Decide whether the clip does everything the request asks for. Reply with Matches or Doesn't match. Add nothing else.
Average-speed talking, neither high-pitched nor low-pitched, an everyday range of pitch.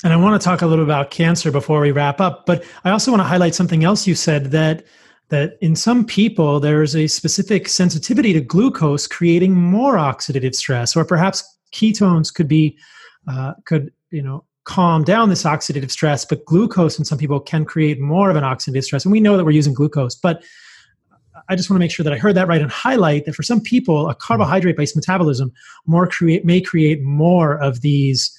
Doesn't match